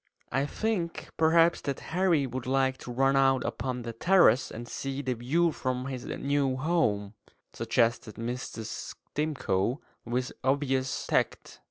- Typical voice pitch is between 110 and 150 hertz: Yes, low, 135 Hz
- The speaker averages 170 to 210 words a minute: No, average, 140 wpm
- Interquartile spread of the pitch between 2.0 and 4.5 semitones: Yes, average, 3.1 semitones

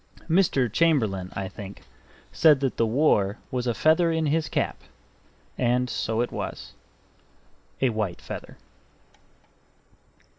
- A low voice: Yes, low, 125 Hz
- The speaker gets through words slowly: Yes, slow, 120 wpm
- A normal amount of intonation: No, wide, 6.4 semitones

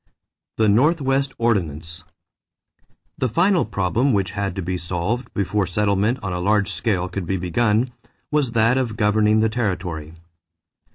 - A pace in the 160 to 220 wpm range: No, average, 145 wpm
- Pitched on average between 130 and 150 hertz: No, low, 105 Hz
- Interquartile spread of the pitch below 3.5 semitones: No, average, 4.5 semitones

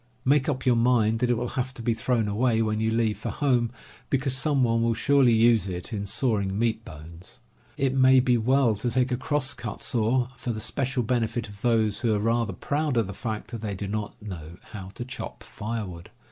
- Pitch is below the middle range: Yes, low, 115 Hz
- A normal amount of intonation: Yes, average, 3.0 semitones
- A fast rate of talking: Yes, fast, 215 wpm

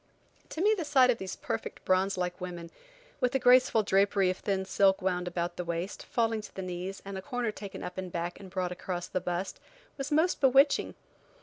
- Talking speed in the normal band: No, fast, 210 wpm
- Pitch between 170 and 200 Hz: Yes, high, 190 Hz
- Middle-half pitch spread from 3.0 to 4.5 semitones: No, average, 5.2 semitones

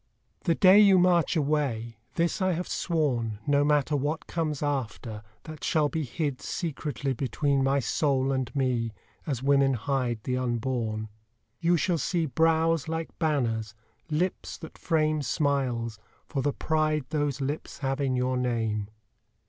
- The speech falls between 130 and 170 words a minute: Yes, average, 150 wpm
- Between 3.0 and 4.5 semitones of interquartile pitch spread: Yes, average, 3.9 semitones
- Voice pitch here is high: No, medium, 140 Hz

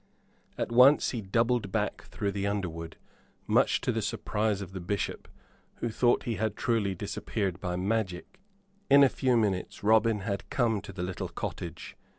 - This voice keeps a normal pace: Yes, average, 165 wpm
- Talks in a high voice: No, low, 105 Hz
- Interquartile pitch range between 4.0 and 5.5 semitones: No, average, 3.4 semitones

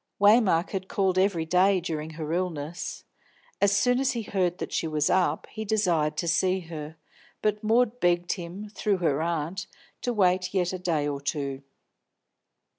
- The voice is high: No, medium, 180 Hz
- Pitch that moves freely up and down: No, average, 3.8 semitones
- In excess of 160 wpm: Yes, average, 170 wpm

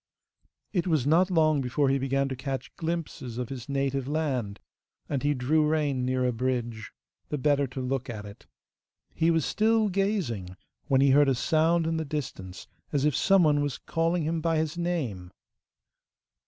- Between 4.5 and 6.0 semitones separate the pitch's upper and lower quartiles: No, average, 4.0 semitones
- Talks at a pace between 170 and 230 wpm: Yes, average, 180 wpm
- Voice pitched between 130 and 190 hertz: Yes, medium, 140 Hz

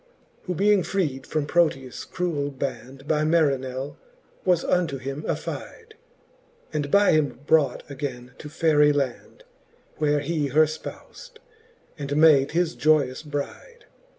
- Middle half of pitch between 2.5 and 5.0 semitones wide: Yes, average, 3.1 semitones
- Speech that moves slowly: Yes, slow, 125 wpm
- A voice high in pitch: No, medium, 150 Hz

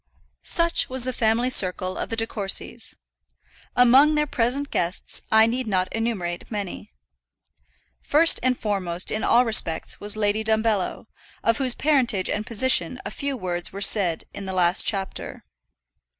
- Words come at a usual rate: Yes, average, 150 wpm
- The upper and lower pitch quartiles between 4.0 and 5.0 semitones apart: Yes, average, 4.7 semitones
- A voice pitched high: Yes, high, 220 Hz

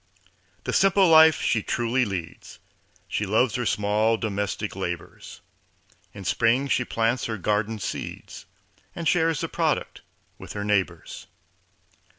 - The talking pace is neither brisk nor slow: No, slow, 130 wpm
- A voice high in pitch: No, low, 110 Hz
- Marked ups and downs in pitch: No, average, 4.0 semitones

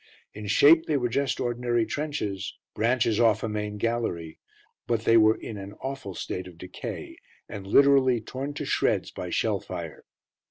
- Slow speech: No, average, 165 wpm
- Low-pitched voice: Yes, low, 115 Hz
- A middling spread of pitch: Yes, average, 4.0 semitones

